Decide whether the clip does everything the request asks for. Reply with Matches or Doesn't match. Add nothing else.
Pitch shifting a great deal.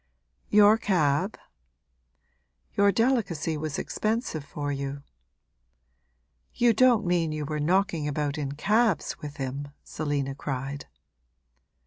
Matches